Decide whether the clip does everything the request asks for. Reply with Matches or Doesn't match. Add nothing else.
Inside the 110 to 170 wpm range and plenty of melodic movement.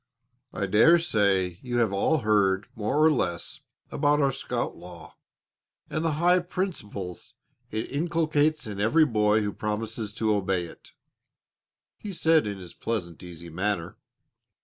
Matches